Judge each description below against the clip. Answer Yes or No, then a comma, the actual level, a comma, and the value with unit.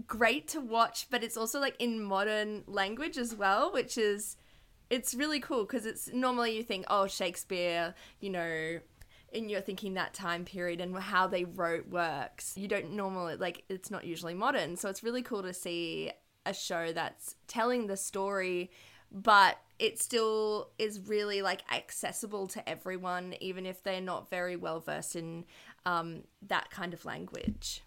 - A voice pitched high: Yes, high, 195 Hz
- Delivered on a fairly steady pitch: No, average, 3.9 semitones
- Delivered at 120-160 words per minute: No, average, 170 wpm